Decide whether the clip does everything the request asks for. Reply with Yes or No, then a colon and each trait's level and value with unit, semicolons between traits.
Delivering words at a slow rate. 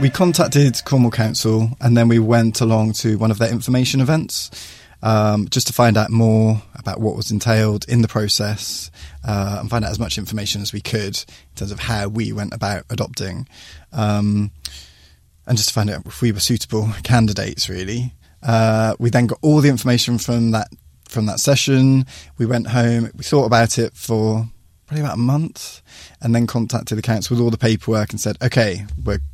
No: average, 195 wpm